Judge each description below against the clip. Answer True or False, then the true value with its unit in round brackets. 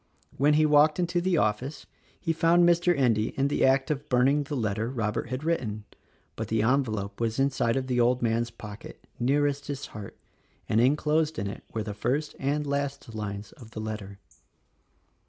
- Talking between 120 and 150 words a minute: False (185 wpm)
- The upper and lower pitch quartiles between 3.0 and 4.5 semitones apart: False (5.0 semitones)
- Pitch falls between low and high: False (130 Hz)